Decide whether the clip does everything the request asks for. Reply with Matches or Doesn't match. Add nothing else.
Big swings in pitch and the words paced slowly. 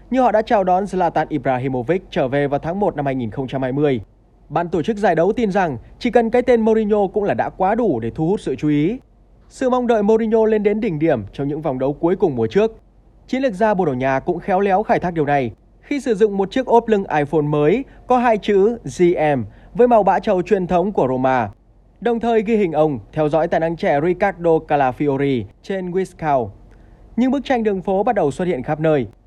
Doesn't match